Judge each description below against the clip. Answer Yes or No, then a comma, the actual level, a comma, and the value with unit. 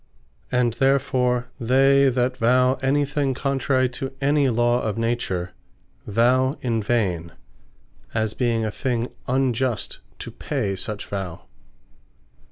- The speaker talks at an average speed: No, slow, 120 wpm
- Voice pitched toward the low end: Yes, low, 125 Hz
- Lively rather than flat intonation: No, average, 2.7 semitones